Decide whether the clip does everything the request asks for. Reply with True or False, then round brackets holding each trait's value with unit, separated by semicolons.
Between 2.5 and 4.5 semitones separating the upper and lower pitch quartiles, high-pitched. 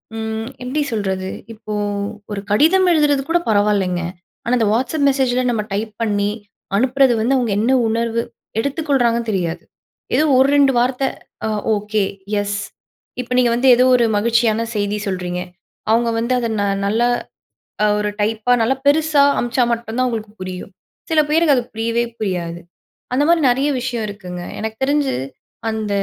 True (3.9 semitones; 230 Hz)